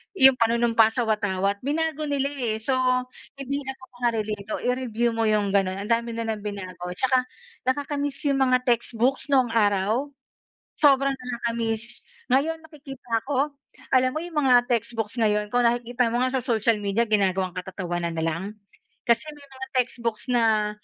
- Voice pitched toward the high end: Yes, high, 235 Hz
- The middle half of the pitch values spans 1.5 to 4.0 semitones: Yes, average, 3.7 semitones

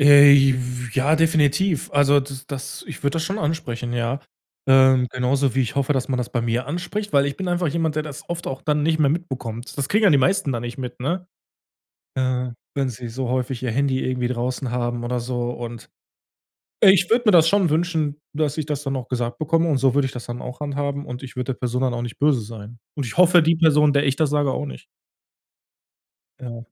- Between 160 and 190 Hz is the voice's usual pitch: No, low, 135 Hz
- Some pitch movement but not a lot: Yes, average, 3.4 semitones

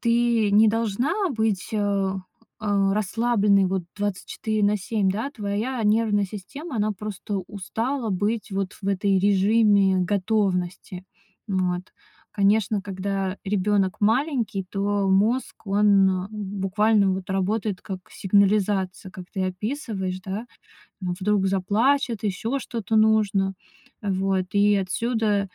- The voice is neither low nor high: No, high, 205 Hz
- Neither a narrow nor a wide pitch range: No, narrow, 2.3 semitones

